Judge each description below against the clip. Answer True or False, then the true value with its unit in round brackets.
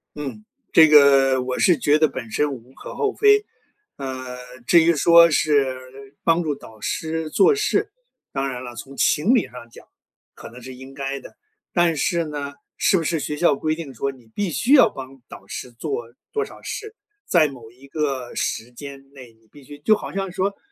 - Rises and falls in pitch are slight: False (4.4 semitones)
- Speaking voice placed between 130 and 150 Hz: True (140 Hz)